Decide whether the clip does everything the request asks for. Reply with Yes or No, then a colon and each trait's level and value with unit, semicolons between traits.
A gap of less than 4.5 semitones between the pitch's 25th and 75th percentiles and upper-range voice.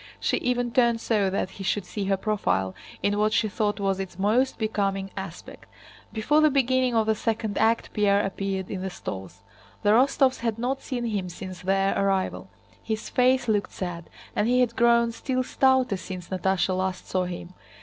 Yes: average, 3.8 semitones; high, 210 Hz